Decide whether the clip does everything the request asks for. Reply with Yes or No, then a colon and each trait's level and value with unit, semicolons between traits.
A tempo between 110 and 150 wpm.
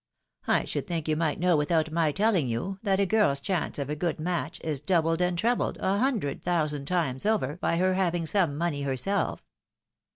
No: average, 200 wpm